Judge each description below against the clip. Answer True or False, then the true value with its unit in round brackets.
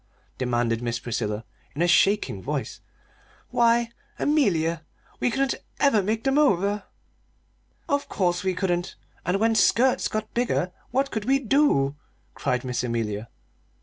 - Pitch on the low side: False (195 Hz)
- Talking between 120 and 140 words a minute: True (135 wpm)